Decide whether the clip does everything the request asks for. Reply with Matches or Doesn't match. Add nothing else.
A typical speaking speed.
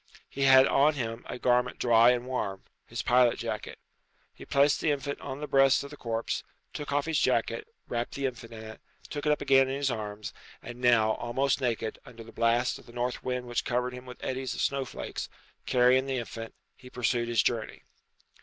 Doesn't match